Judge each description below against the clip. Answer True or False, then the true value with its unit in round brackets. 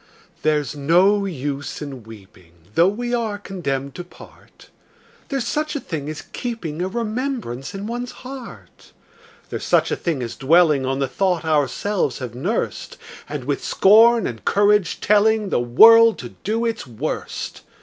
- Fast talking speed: False (155 wpm)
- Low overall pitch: False (180 Hz)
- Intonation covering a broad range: True (8.2 semitones)